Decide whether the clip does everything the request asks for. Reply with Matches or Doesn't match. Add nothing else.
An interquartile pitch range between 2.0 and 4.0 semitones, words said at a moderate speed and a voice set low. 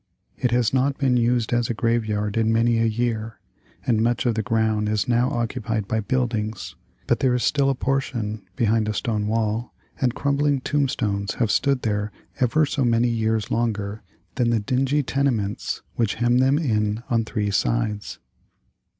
Matches